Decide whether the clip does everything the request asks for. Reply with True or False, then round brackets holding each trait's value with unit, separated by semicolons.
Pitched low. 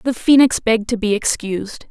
False (225 Hz)